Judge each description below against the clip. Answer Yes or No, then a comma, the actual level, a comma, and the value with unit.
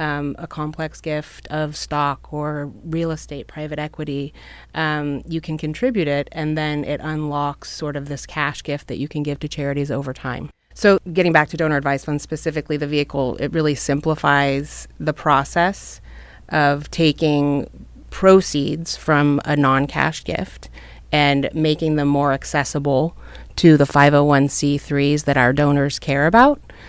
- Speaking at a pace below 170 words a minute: Yes, average, 155 wpm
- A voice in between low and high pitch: Yes, medium, 150 Hz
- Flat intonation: Yes, narrow, 1.5 semitones